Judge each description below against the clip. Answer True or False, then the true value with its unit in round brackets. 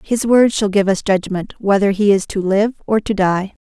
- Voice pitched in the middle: False (200 Hz)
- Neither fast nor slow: False (230 wpm)